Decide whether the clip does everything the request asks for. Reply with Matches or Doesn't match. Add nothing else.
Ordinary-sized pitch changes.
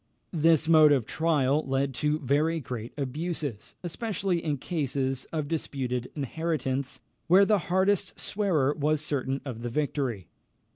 Matches